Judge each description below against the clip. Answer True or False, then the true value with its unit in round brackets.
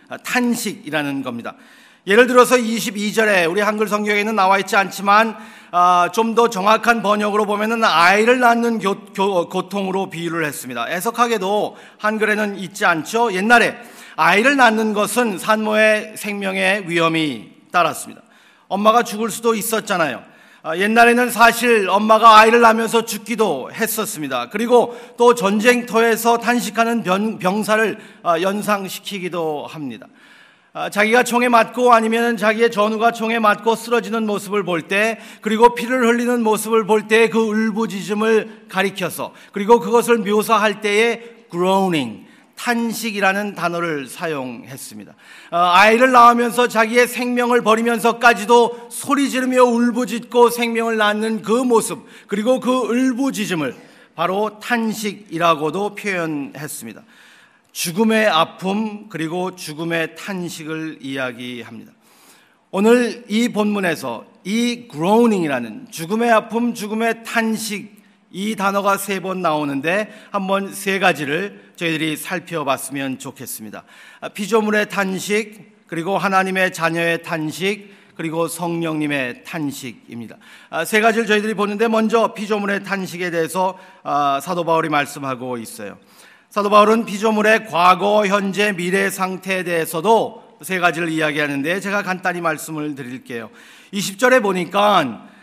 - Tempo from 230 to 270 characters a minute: False (310 characters per minute)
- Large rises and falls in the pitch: False (4.1 semitones)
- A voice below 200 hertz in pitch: False (210 Hz)